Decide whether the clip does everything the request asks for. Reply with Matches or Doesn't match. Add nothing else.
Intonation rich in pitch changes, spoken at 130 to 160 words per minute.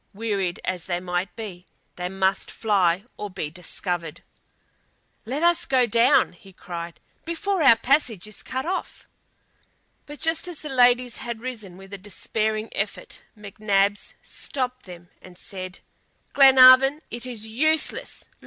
Matches